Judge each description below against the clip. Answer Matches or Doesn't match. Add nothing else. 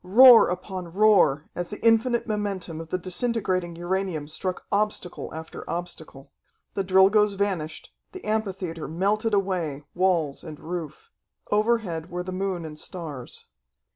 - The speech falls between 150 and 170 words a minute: Doesn't match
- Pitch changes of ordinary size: Matches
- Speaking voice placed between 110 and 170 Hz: Doesn't match